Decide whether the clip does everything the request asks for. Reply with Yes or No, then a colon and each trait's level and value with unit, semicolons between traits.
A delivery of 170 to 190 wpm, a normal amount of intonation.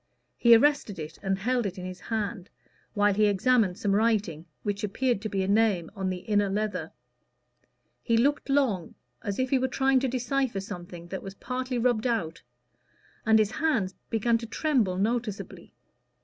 Yes: average, 175 wpm; average, 4.2 semitones